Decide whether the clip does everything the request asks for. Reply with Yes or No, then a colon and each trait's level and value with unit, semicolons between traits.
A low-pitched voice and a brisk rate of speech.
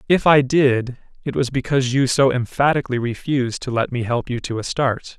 Yes: low, 130 Hz; fast, 210 wpm